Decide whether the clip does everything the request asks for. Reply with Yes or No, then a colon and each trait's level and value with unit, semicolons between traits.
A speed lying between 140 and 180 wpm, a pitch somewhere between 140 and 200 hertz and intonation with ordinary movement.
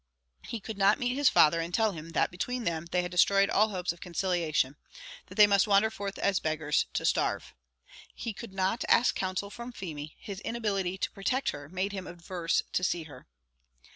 No: average, 200 wpm; high, 190 Hz; average, 3.5 semitones